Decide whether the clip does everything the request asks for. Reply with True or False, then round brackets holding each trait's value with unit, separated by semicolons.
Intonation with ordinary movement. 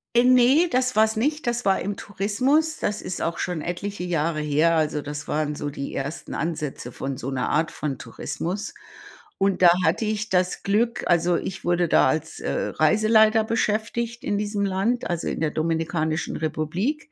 False (5.7 semitones)